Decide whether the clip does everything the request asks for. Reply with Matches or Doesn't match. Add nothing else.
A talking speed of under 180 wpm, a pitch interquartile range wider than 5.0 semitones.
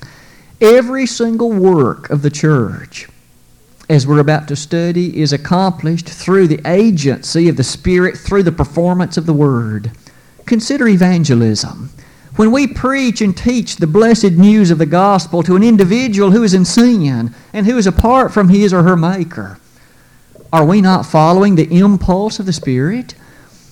Matches